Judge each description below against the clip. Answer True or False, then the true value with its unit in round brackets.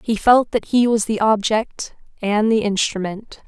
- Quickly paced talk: False (170 wpm)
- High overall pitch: True (215 Hz)